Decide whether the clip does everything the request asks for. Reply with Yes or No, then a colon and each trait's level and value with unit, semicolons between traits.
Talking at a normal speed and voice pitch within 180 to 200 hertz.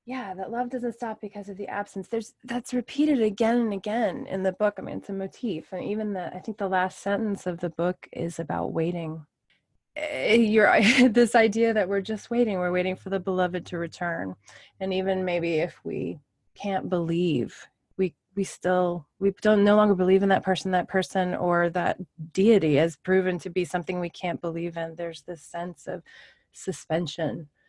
Yes: average, 190 wpm; high, 190 Hz